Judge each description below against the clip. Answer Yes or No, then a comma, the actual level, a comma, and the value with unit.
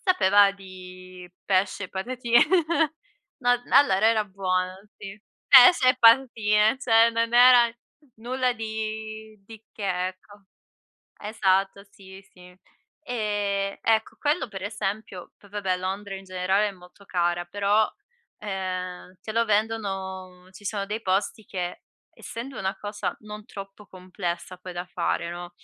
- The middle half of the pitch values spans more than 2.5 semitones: Yes, average, 2.9 semitones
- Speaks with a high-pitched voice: Yes, high, 200 Hz